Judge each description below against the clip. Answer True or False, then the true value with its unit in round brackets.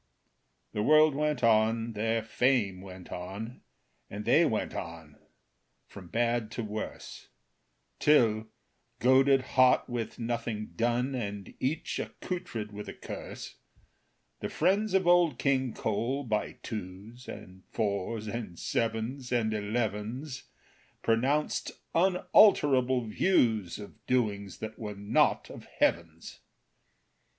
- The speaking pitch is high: False (115 Hz)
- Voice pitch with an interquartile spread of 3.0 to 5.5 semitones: True (3.8 semitones)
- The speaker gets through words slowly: True (115 wpm)